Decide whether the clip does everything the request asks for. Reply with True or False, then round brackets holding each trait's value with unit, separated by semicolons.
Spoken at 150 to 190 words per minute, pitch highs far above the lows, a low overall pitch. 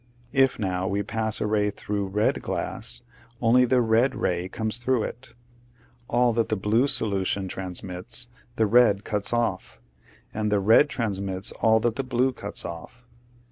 False (160 wpm; 3.4 semitones; 110 Hz)